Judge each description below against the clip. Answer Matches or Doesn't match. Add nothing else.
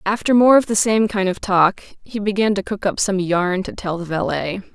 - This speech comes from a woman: Matches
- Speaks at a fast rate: Matches